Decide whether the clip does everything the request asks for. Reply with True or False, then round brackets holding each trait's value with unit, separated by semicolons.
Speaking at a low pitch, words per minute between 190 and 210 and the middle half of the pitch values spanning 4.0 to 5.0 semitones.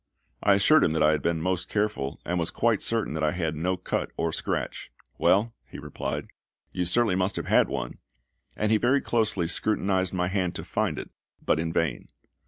True (90 Hz; 200 wpm; 4.4 semitones)